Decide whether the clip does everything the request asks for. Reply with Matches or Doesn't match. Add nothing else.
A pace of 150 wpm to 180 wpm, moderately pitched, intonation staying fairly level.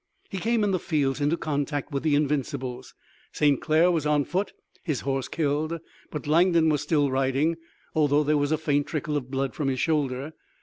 Doesn't match